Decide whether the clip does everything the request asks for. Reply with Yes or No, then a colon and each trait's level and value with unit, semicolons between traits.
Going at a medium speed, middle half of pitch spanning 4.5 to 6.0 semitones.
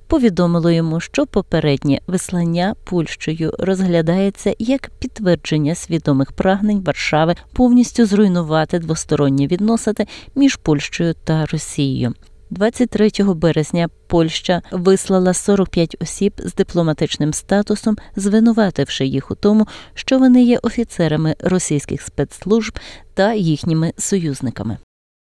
No: slow, 100 wpm; average, 5.1 semitones